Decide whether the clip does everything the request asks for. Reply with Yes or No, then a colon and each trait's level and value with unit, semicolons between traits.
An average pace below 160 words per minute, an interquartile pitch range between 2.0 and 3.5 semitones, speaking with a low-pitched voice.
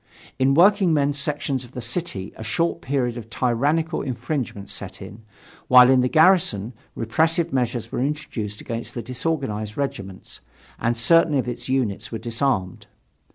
No: average, 150 wpm; average, 4.7 semitones; low, 125 Hz